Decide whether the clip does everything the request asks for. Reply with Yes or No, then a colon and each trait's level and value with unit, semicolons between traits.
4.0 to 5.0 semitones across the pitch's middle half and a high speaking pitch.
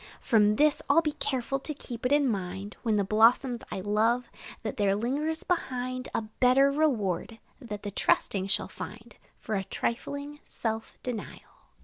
Yes: average, 4.6 semitones; high, 235 Hz